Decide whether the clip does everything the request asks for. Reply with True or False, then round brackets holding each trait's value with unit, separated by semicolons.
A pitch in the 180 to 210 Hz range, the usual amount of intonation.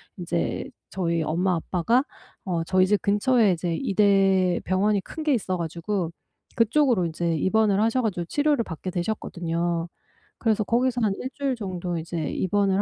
True (190 Hz; 4.2 semitones)